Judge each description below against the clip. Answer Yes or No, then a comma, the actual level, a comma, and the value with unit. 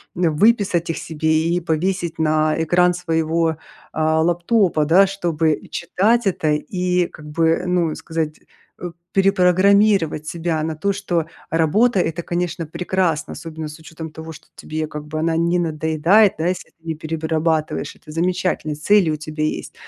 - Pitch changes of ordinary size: No, narrow, 2.3 semitones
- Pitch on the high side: No, medium, 165 Hz